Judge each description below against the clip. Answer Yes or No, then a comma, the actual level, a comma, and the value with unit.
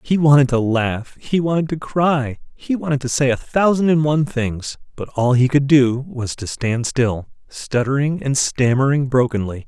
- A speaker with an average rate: Yes, average, 185 wpm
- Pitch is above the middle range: No, low, 135 Hz